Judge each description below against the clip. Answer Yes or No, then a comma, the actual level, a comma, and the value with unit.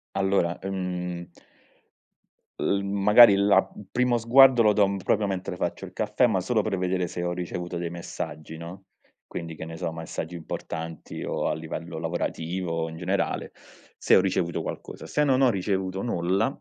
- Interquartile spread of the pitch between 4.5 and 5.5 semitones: No, average, 2.8 semitones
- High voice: No, very low, 95 Hz